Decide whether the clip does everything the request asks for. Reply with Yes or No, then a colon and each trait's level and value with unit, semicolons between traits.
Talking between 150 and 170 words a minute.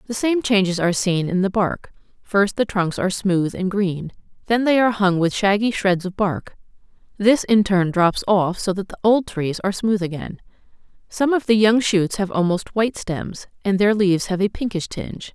No: fast, 205 wpm